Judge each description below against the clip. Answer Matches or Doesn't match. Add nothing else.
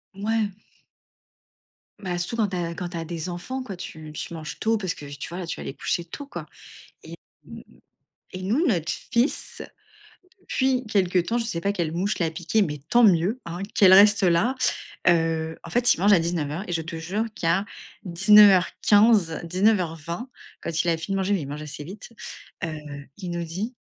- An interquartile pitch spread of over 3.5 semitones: Matches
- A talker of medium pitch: Matches